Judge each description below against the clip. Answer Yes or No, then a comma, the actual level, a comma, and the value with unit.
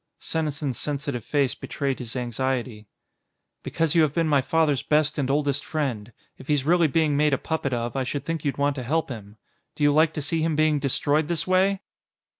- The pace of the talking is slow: No, fast, 205 wpm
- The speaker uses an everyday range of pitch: Yes, average, 3.0 semitones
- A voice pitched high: No, medium, 145 Hz